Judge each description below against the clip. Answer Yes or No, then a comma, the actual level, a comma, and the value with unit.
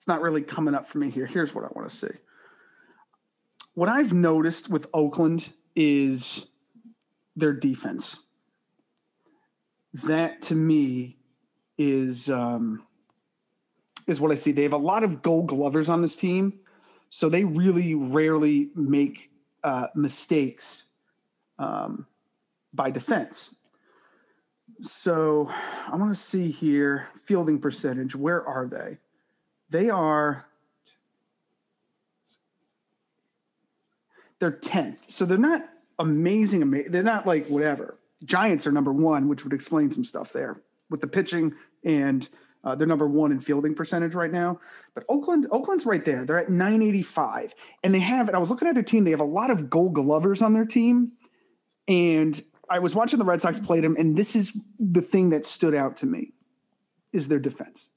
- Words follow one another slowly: No, average, 155 wpm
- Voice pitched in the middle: Yes, medium, 170 Hz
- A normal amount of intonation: No, wide, 6.0 semitones